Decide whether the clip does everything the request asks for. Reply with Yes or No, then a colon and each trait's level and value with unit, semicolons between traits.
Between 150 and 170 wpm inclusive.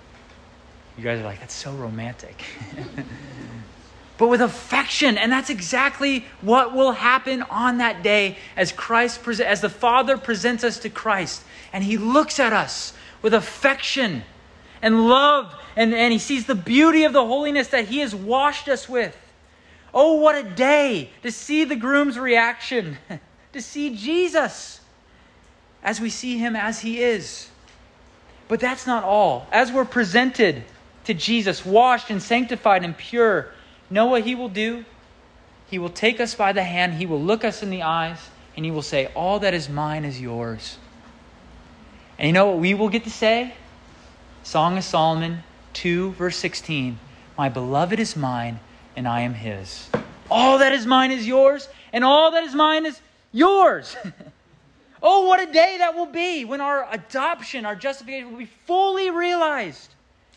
Yes: average, 165 wpm